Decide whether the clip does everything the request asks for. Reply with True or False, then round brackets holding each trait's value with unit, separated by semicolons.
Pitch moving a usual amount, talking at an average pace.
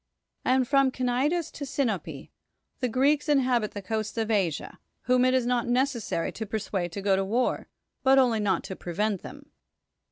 True (4.0 semitones; 170 wpm)